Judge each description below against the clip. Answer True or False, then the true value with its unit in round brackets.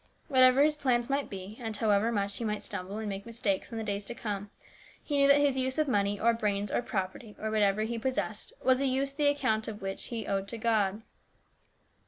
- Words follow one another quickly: True (230 wpm)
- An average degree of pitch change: True (4.2 semitones)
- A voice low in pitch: False (220 Hz)